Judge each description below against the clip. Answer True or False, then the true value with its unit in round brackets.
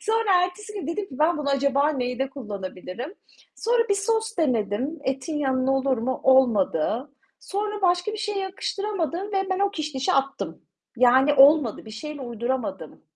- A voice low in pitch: False (290 Hz)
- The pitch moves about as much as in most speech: False (6.9 semitones)